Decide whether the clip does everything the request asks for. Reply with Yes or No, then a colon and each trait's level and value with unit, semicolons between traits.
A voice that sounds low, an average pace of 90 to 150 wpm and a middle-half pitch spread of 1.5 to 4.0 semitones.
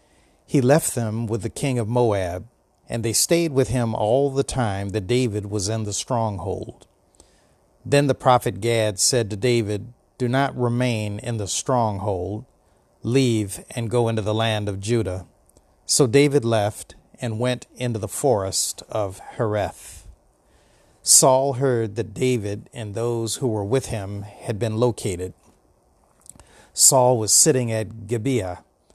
Yes: low, 115 Hz; average, 145 wpm; average, 3.1 semitones